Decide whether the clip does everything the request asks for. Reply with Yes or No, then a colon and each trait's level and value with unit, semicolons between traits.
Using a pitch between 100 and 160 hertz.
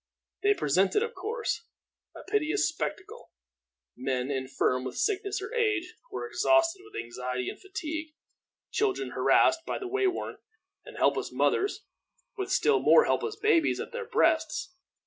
No: very high, 380 Hz